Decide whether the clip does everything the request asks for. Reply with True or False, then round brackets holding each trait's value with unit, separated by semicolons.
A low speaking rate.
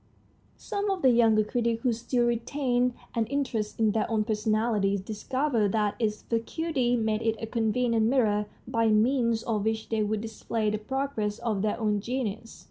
False (170 wpm)